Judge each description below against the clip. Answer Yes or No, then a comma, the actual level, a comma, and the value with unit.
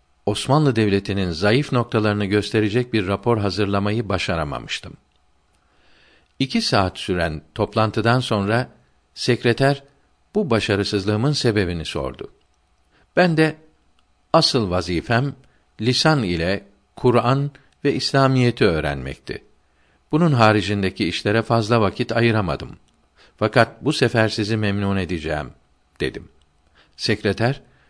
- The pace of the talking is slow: Yes, slow, 90 wpm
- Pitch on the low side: Yes, low, 105 Hz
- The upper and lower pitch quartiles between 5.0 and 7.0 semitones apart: Yes, wide, 5.5 semitones